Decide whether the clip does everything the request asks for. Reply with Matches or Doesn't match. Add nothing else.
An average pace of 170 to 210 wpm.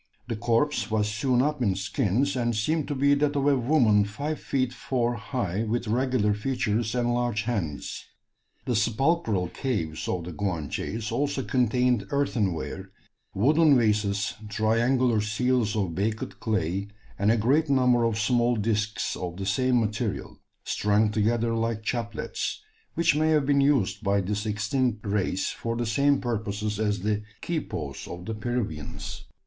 Doesn't match